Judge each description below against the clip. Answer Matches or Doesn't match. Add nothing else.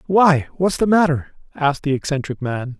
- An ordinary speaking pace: Matches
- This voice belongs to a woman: Doesn't match